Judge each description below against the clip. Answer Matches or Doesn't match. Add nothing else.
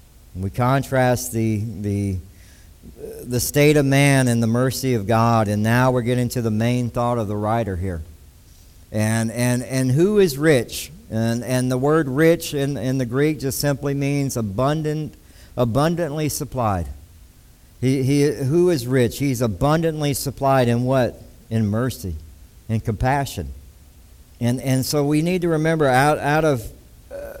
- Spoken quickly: Doesn't match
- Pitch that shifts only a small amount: Doesn't match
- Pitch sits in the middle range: Doesn't match